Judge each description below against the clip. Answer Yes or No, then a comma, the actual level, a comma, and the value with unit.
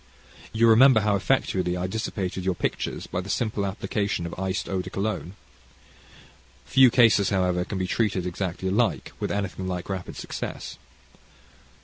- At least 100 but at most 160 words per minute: Yes, average, 150 wpm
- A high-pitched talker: No, very low, 95 Hz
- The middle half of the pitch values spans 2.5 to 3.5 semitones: Yes, average, 2.9 semitones